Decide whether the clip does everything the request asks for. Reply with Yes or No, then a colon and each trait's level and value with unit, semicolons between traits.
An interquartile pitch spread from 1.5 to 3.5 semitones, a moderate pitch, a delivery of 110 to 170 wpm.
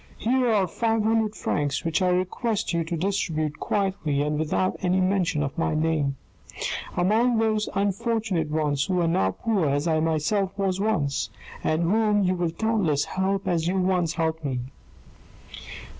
No: average, 4.4 semitones; medium, 180 Hz; average, 160 wpm